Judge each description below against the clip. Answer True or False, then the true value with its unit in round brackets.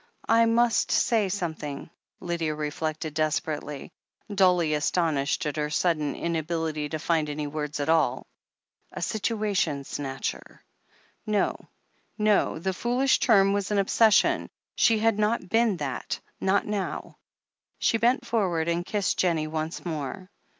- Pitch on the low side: False (170 Hz)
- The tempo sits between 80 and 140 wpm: True (135 wpm)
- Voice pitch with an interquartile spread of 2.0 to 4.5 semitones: False (5.2 semitones)